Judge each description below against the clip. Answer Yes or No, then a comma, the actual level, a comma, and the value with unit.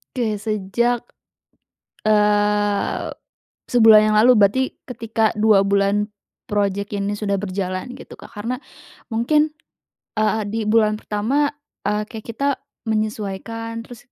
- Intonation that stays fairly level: Yes, narrow, 1.8 semitones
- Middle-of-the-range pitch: No, high, 215 Hz